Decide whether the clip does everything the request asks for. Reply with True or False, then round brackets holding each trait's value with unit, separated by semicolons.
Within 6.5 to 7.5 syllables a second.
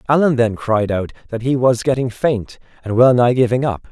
False (5.1 syllables/s)